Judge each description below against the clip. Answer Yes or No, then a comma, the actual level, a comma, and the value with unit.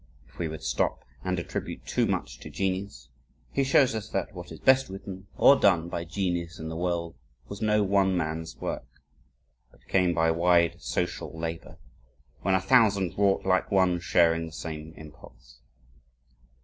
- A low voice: Yes, very low, 90 Hz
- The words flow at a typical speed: Yes, average, 165 wpm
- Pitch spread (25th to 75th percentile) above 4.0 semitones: No, average, 3.0 semitones